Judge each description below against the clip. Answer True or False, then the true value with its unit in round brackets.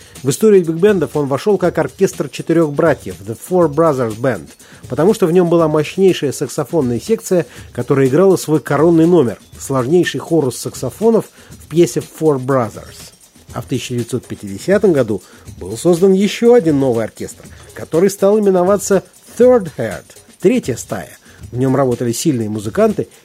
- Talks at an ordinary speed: True (140 wpm)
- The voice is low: False (155 Hz)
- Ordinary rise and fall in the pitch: False (6.5 semitones)